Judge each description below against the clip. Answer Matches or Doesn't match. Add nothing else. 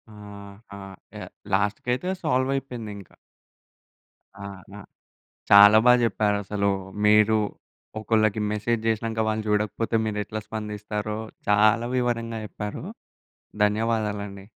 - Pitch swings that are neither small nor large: Doesn't match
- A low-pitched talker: Matches